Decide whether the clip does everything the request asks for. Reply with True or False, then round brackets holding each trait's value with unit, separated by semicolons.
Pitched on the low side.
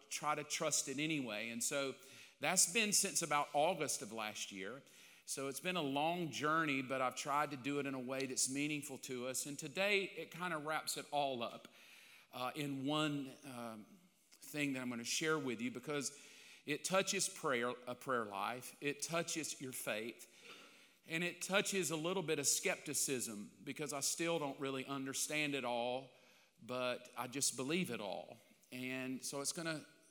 False (145 Hz)